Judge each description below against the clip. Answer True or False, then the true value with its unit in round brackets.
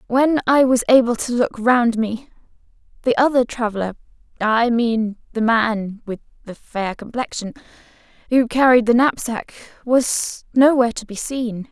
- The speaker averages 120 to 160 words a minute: True (135 wpm)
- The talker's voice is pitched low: False (235 Hz)